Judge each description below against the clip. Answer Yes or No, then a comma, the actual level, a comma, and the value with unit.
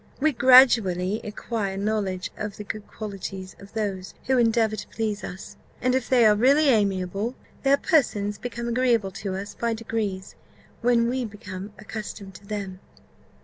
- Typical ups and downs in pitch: Yes, average, 3.2 semitones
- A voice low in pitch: No, high, 215 Hz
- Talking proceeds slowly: No, average, 155 wpm